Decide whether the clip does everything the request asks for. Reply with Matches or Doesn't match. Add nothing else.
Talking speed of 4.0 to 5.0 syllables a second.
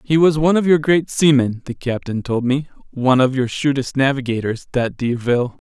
Doesn't match